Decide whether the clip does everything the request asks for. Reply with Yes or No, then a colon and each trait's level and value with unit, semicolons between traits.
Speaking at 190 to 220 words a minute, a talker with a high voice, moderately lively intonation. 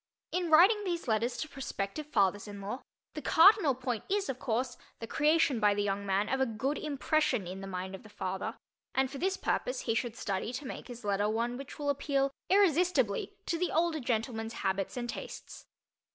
No: average, 200 wpm; very high, 250 Hz; wide, 6.7 semitones